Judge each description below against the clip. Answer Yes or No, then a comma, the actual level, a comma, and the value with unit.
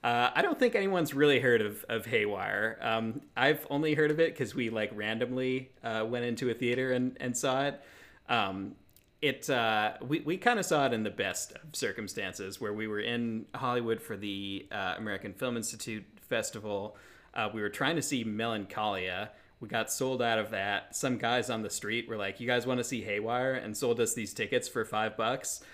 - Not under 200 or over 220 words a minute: Yes, fast, 205 wpm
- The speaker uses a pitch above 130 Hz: No, low, 120 Hz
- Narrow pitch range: No, average, 3.5 semitones